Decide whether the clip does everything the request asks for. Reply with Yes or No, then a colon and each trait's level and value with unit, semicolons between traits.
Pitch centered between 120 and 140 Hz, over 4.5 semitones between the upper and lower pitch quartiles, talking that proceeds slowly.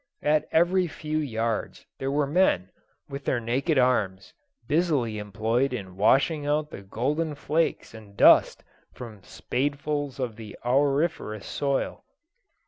Yes: low, 135 Hz; average, 5.2 semitones; slow, 130 wpm